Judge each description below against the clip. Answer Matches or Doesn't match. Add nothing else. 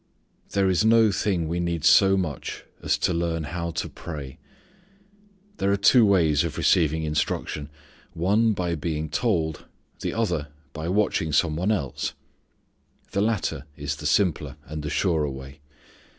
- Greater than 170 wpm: Doesn't match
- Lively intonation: Doesn't match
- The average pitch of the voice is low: Matches